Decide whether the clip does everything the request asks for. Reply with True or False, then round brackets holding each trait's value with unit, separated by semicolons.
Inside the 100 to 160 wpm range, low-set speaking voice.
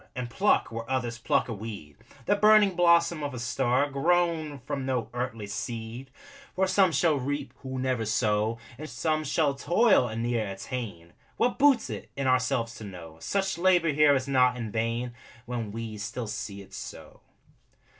False (175 wpm; 125 Hz)